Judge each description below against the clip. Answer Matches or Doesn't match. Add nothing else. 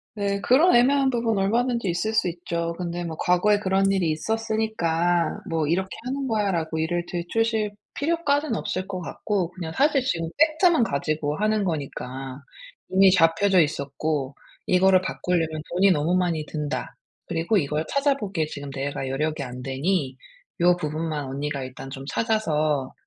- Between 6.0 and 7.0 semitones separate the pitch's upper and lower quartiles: Doesn't match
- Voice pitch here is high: Doesn't match